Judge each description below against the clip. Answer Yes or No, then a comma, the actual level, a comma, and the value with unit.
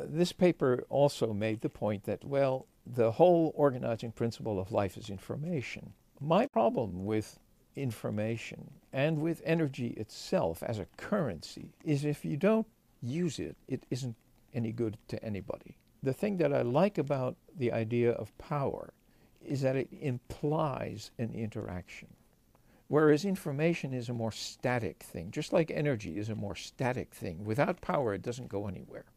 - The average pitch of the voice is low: Yes, low, 125 Hz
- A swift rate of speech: No, average, 155 wpm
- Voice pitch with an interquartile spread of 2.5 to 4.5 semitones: No, average, 5.2 semitones